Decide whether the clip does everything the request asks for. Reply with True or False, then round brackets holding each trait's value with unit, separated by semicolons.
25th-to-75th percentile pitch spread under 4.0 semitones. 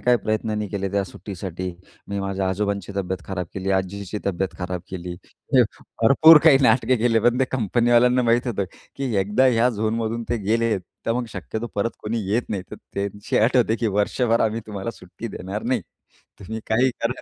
True (3.3 semitones)